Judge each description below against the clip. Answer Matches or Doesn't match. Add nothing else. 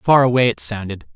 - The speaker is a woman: Doesn't match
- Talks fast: Matches